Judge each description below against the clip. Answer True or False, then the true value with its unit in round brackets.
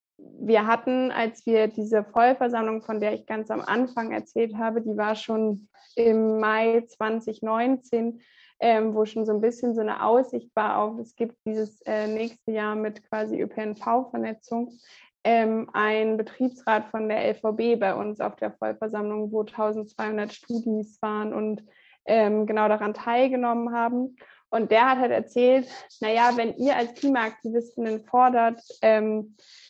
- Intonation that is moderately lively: False (1.6 semitones)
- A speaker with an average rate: True (150 wpm)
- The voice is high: True (225 Hz)